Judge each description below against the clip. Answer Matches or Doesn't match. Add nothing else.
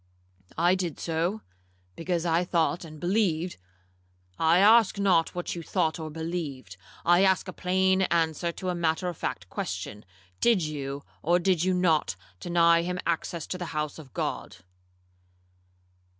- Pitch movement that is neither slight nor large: Doesn't match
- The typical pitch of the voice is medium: Matches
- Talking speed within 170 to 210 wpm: Doesn't match